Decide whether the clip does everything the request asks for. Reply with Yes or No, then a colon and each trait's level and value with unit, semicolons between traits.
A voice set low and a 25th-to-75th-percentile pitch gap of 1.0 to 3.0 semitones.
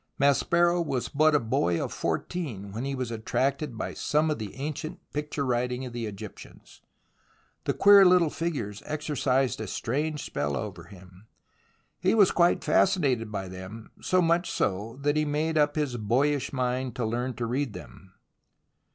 No: low, 130 Hz; wide, 5.6 semitones